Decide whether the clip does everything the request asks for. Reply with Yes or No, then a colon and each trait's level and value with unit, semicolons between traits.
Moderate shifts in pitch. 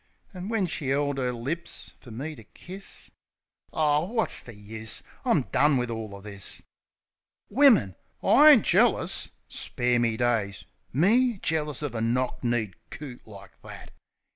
No: wide, 6.7 semitones